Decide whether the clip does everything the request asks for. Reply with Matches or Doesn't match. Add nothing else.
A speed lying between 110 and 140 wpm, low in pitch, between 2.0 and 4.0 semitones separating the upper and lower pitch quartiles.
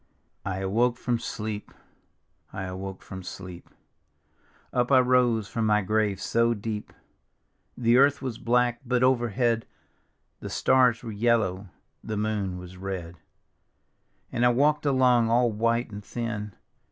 Matches